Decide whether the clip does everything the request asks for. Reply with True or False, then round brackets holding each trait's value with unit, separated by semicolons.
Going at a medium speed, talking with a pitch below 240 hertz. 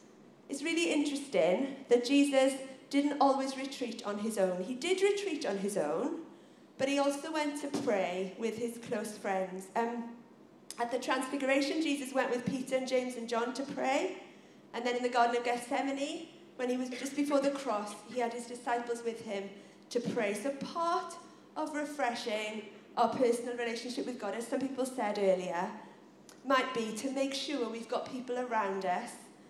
False (175 wpm; 250 Hz)